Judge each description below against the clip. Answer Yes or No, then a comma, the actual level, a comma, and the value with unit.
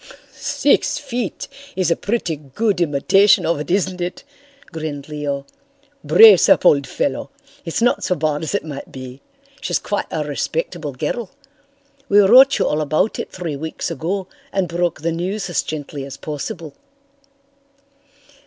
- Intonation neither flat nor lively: Yes, average, 4.6 semitones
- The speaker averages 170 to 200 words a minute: No, average, 155 wpm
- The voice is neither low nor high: Yes, medium, 165 Hz